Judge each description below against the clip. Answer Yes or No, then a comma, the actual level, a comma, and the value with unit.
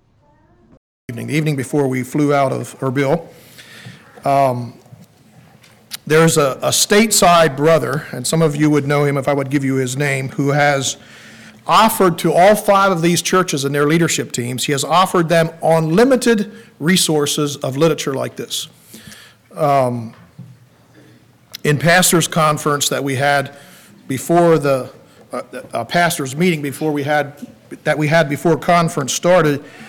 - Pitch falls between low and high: Yes, medium, 150 Hz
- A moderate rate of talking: Yes, average, 150 wpm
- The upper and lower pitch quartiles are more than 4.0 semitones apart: No, average, 3.2 semitones